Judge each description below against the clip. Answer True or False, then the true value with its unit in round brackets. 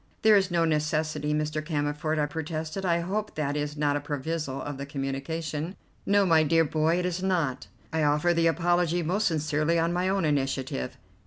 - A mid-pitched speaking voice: True (155 Hz)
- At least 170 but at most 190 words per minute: True (185 wpm)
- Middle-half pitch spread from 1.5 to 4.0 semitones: True (2.7 semitones)